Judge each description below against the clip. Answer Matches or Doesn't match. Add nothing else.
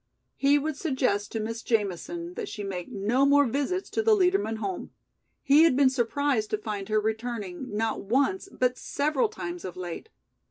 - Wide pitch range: Matches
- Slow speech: Doesn't match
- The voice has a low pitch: Doesn't match